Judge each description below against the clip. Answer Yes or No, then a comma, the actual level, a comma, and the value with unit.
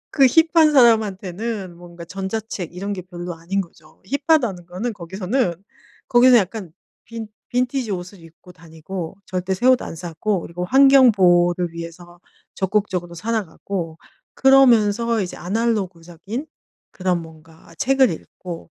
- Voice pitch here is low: No, high, 190 Hz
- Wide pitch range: No, average, 4.9 semitones